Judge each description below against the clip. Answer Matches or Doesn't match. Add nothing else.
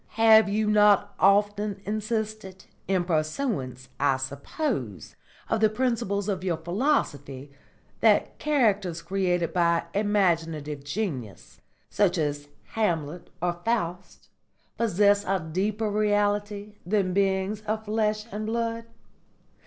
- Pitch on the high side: Matches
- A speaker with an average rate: Doesn't match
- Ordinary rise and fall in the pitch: Matches